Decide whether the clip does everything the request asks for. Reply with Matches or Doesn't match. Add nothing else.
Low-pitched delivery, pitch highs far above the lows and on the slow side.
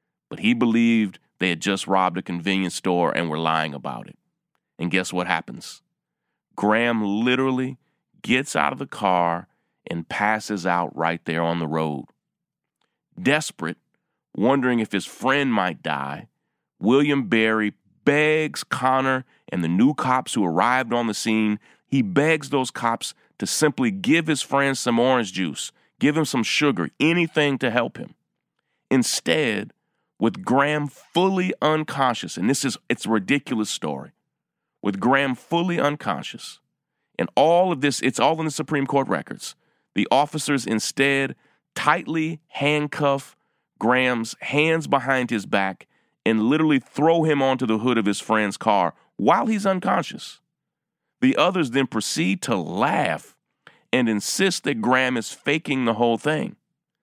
Doesn't match